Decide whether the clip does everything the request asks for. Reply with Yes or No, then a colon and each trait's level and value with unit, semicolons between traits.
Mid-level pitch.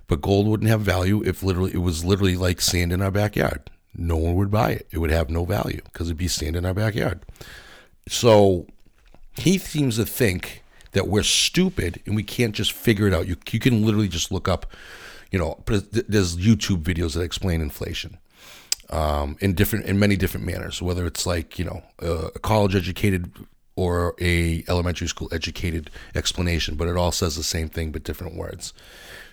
No: very low, 90 Hz